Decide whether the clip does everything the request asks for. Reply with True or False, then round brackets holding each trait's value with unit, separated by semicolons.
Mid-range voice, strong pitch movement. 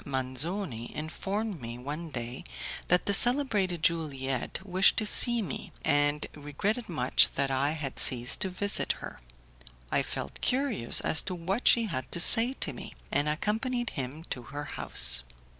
True (160 Hz; 7.3 semitones)